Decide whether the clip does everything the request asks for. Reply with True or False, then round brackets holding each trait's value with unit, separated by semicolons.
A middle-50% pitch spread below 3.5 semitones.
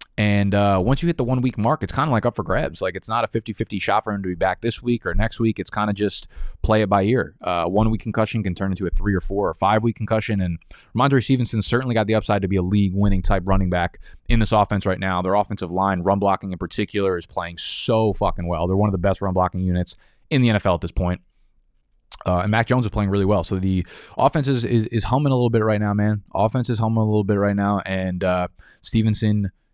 True (2.9 semitones)